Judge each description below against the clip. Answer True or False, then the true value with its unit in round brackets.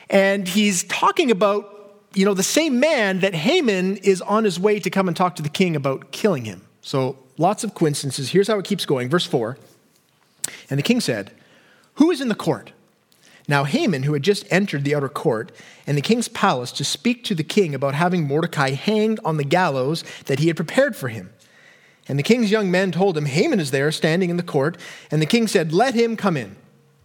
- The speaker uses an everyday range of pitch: False (5.7 semitones)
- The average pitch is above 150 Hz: True (185 Hz)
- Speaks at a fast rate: True (215 wpm)